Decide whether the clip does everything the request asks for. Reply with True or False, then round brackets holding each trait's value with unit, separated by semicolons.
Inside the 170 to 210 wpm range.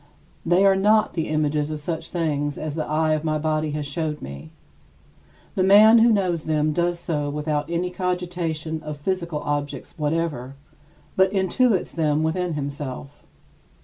False (155 wpm)